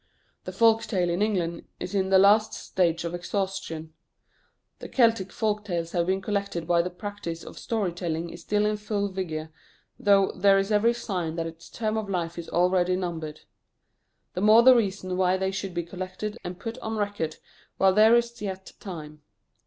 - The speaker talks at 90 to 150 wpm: No, average, 185 wpm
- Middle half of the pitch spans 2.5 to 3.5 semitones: Yes, average, 3.2 semitones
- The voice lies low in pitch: No, high, 190 Hz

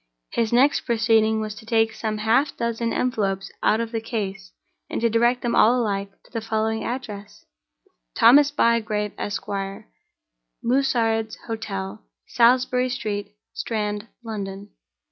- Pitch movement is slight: Yes, narrow, 2.0 semitones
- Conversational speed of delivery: No, slow, 130 wpm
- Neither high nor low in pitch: No, high, 225 Hz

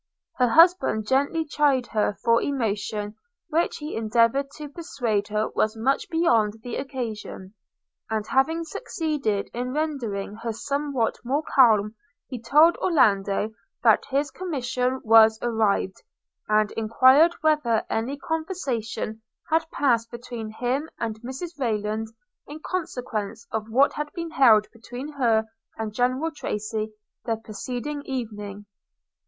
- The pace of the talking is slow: Yes, slow, 125 wpm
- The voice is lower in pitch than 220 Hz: No, high, 245 Hz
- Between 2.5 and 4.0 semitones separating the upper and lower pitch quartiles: No, average, 4.7 semitones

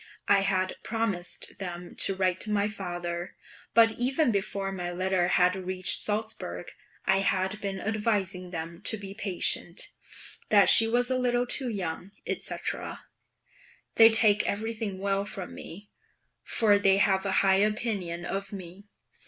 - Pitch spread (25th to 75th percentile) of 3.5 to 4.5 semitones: No, narrow, 2.6 semitones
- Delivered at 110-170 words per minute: Yes, average, 145 wpm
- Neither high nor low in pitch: No, high, 195 Hz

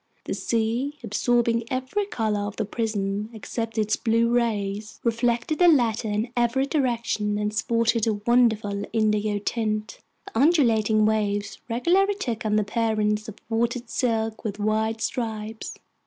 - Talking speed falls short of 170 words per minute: Yes, average, 140 wpm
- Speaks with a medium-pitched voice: No, high, 225 Hz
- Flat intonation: Yes, narrow, 2.1 semitones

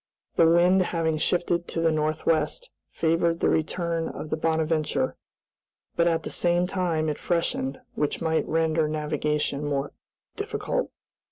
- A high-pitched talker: No, medium, 160 Hz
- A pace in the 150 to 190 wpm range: No, average, 140 wpm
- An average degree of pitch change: No, narrow, 1.6 semitones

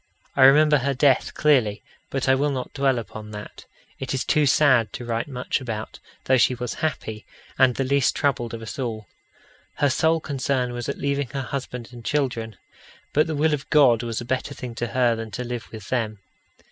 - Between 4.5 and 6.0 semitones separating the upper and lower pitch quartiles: No, average, 3.2 semitones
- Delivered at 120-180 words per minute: No, fast, 205 wpm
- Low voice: Yes, low, 130 Hz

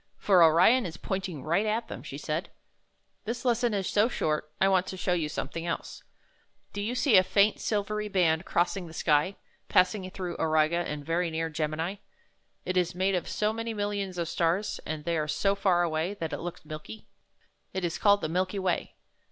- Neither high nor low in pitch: Yes, medium, 180 Hz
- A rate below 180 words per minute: No, average, 195 wpm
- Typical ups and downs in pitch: Yes, average, 3.8 semitones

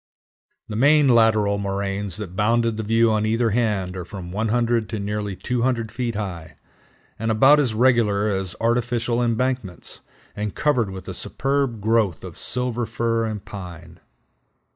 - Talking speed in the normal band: Yes, average, 150 wpm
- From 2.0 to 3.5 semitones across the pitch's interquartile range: Yes, average, 2.9 semitones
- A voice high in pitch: No, low, 110 Hz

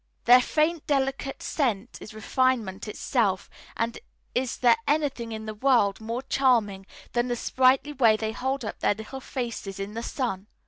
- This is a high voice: Yes, high, 240 Hz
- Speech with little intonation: No, average, 3.6 semitones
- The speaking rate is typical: Yes, average, 165 wpm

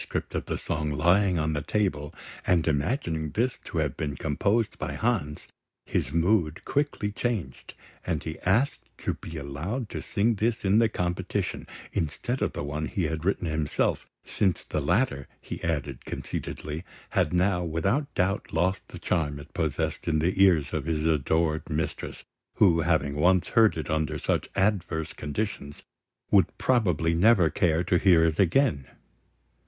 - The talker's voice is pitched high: No, very low, 85 Hz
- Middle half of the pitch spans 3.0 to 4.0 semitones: No, average, 4.5 semitones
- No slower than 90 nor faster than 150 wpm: No, average, 160 wpm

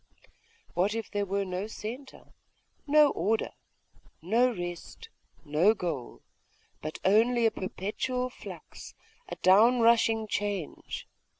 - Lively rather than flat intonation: No, average, 4.1 semitones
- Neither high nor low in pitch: No, high, 215 Hz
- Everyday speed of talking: No, slow, 110 wpm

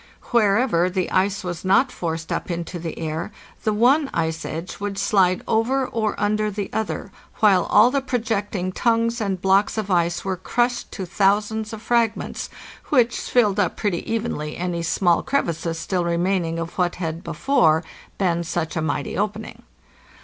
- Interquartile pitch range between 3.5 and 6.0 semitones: Yes, average, 4.3 semitones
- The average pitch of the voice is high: Yes, high, 195 Hz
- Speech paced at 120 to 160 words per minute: No, average, 175 wpm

